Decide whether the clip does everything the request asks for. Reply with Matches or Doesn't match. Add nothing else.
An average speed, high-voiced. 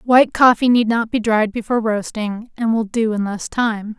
Doesn't match